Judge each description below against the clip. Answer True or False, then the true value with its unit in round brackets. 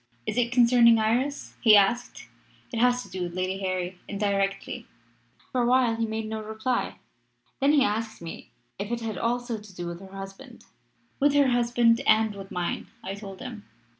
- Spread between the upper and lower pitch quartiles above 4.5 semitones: False (3.7 semitones)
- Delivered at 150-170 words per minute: False (185 wpm)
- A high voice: True (220 Hz)